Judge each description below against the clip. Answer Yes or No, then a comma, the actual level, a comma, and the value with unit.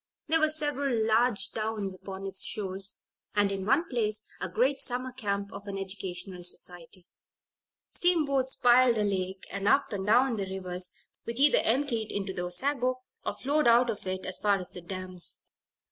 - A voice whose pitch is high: Yes, high, 210 Hz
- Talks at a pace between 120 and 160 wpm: No, average, 175 wpm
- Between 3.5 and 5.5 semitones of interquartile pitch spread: Yes, average, 4.9 semitones